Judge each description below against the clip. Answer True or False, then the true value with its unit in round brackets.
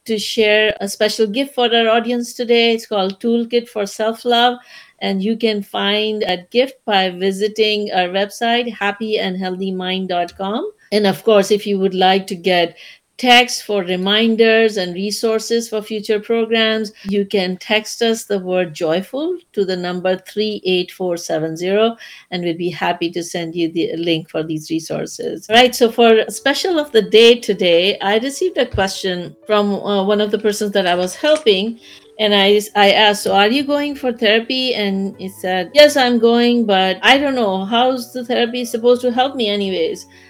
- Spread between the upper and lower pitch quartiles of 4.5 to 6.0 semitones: False (3.6 semitones)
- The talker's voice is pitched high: True (210 Hz)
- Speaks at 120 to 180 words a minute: True (175 wpm)